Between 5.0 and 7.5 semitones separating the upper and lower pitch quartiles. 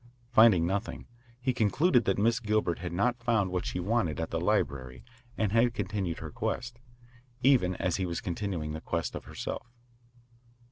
Yes: average, 5.3 semitones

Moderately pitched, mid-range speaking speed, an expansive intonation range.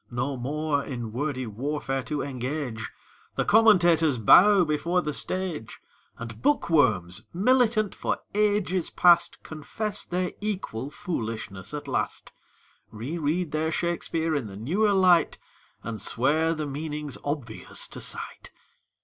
No: medium, 150 Hz; slow, 125 wpm; wide, 5.8 semitones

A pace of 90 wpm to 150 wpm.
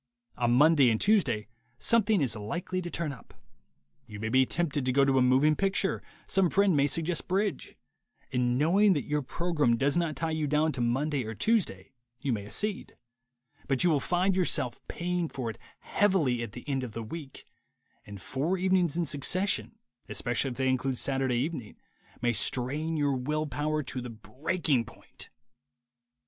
No: average, 180 wpm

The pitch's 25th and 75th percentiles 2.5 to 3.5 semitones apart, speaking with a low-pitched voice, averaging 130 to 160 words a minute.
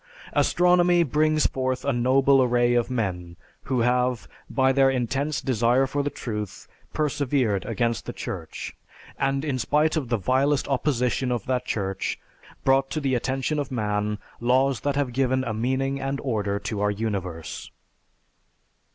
Yes: average, 3.0 semitones; low, 130 Hz; average, 150 wpm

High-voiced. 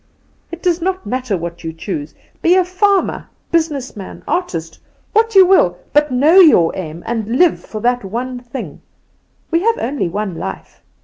Yes: very high, 255 Hz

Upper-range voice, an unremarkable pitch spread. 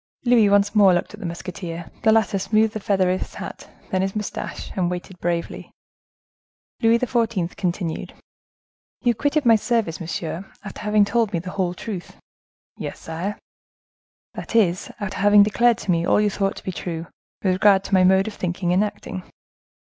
Yes: high, 195 Hz; average, 3.0 semitones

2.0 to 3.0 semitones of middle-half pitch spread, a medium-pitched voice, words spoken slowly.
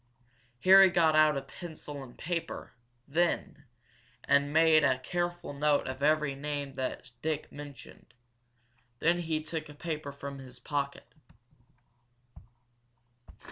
Yes: narrow, 2.4 semitones; medium, 150 Hz; slow, 120 wpm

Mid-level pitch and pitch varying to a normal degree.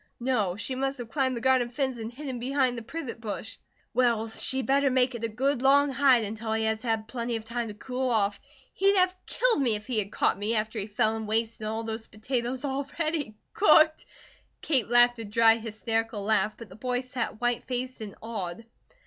No: high, 235 Hz; average, 3.0 semitones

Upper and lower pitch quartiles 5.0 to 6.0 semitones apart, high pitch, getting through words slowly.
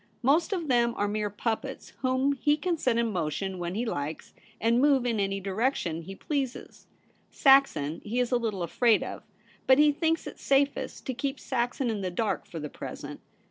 No: wide, 5.6 semitones; high, 235 Hz; average, 195 wpm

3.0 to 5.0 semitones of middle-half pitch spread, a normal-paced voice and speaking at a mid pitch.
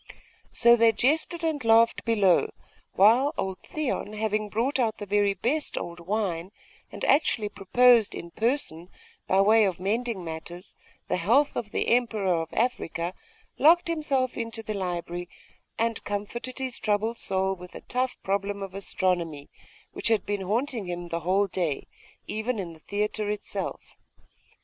No: average, 4.2 semitones; average, 155 wpm; high, 210 Hz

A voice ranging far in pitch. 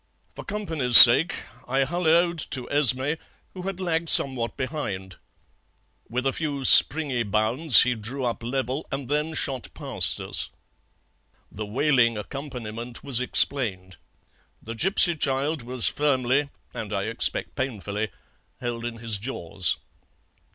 No: average, 4.2 semitones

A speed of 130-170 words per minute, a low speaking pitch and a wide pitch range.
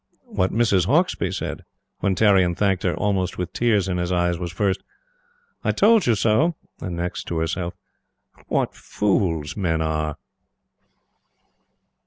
No: average, 140 wpm; very low, 95 Hz; average, 3.2 semitones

